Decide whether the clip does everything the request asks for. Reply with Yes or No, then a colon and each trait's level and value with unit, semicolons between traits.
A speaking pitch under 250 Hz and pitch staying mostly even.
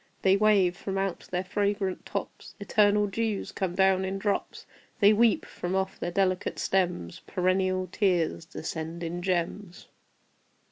Yes: high, 190 Hz; narrow, 2.1 semitones